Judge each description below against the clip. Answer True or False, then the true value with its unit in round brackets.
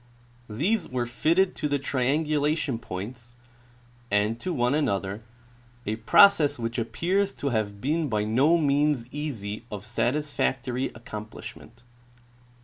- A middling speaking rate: False (125 wpm)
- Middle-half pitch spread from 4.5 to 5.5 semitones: True (5.2 semitones)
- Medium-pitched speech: False (130 Hz)